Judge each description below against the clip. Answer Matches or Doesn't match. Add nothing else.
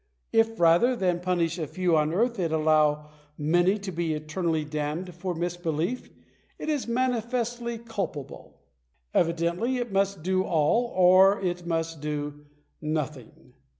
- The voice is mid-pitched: Matches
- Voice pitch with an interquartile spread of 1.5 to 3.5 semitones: Doesn't match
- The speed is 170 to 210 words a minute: Doesn't match